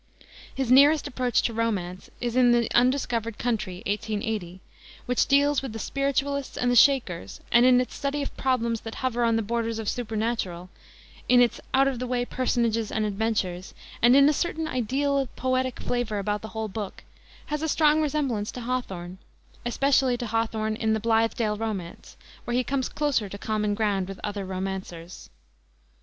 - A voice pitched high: Yes, high, 235 Hz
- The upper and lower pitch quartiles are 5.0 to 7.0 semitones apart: No, average, 3.4 semitones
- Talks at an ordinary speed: Yes, average, 175 wpm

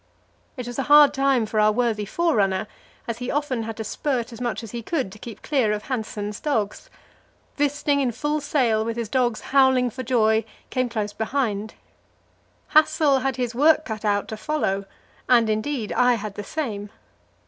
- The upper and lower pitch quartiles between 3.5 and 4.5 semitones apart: Yes, average, 4.1 semitones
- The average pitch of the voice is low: No, high, 240 Hz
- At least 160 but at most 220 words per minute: Yes, average, 180 wpm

